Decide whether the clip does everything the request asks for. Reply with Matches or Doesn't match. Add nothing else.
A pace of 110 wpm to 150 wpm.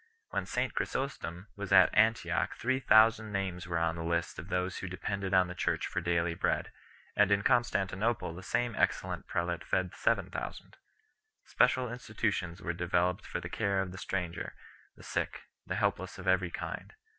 Doesn't match